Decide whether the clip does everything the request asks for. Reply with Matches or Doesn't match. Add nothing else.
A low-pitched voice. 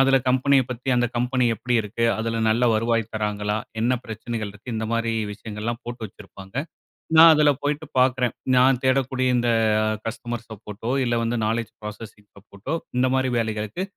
Matches